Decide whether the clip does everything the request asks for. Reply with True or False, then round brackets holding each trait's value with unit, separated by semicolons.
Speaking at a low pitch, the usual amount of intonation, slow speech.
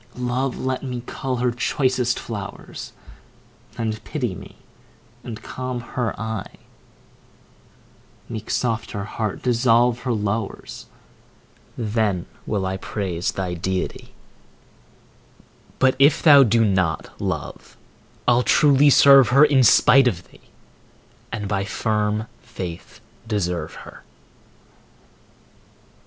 True (115 Hz; 3.9 semitones; 110 wpm)